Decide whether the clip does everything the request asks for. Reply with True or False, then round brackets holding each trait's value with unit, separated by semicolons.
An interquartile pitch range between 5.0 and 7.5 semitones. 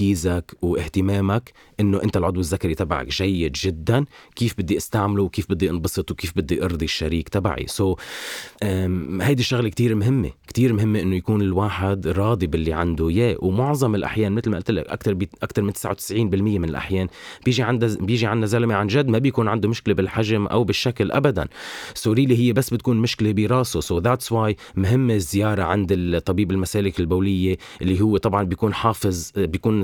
False (3.4 semitones)